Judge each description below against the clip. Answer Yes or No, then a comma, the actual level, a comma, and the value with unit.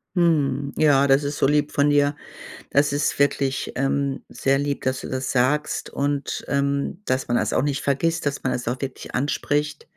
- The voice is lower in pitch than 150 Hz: Yes, medium, 140 Hz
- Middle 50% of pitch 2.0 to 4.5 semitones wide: No, narrow, 1.4 semitones